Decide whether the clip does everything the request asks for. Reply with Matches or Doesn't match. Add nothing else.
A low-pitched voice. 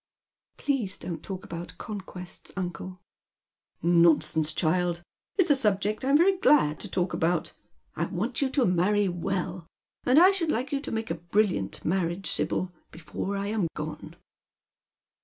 Doesn't match